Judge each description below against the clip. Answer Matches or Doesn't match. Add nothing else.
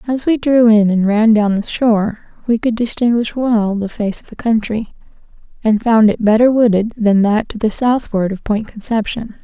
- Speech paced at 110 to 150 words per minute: Doesn't match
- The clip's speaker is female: Matches